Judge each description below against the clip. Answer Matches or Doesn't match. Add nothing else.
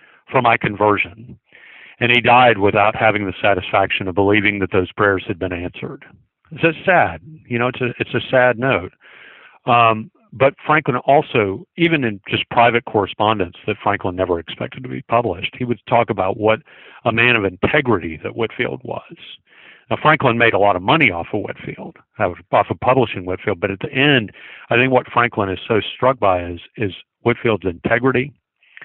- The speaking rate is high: Doesn't match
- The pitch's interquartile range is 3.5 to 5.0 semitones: Matches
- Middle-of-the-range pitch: Doesn't match